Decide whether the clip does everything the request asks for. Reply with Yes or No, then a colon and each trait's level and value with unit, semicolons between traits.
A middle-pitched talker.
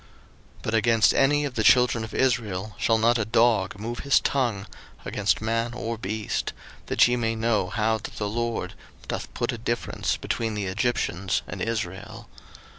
No: low, 115 Hz